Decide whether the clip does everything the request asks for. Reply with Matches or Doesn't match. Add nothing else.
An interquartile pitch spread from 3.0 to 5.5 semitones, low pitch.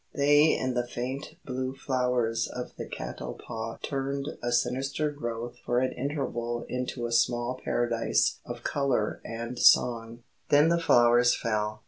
Doesn't match